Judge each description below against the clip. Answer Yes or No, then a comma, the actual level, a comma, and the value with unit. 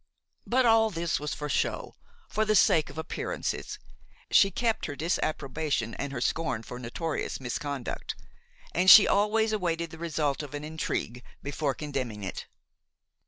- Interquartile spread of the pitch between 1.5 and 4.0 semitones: No, average, 4.8 semitones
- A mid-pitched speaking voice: Yes, medium, 155 Hz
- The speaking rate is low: No, average, 150 wpm